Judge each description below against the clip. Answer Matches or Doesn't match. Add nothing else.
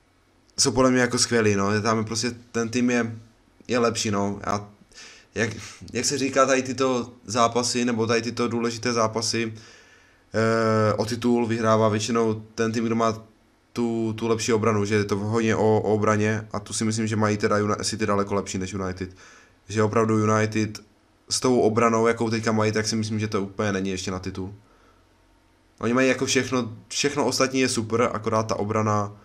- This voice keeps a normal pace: Doesn't match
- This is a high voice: Doesn't match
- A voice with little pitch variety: Matches